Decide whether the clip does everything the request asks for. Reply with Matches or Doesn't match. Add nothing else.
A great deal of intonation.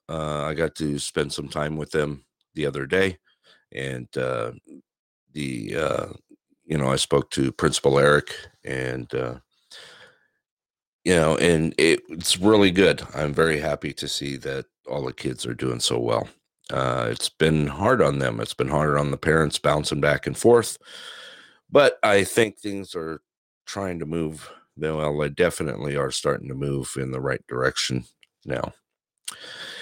Doesn't match